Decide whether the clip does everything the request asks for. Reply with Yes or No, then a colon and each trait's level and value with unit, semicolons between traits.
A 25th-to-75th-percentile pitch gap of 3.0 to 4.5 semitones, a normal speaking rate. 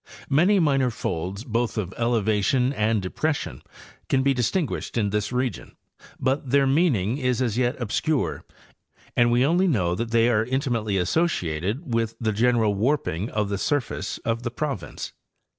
Yes: average, 4.2 semitones; average, 160 wpm